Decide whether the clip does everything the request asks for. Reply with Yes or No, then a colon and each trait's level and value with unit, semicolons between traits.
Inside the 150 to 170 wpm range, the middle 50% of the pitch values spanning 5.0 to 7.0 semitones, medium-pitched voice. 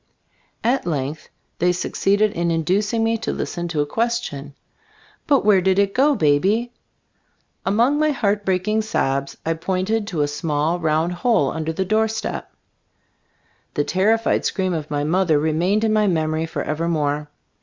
Yes: average, 160 wpm; wide, 5.5 semitones; medium, 180 Hz